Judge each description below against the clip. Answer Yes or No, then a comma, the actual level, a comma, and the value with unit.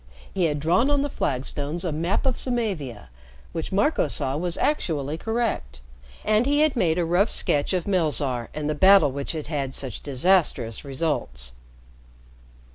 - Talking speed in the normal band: Yes, average, 160 wpm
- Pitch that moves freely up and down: Yes, wide, 6.0 semitones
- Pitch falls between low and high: Yes, medium, 160 Hz